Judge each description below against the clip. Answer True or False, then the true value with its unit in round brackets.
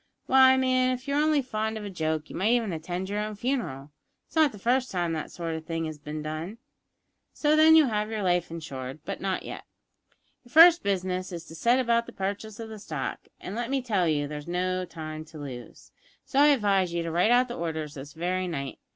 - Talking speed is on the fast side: True (230 wpm)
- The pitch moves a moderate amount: False (6.9 semitones)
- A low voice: False (190 Hz)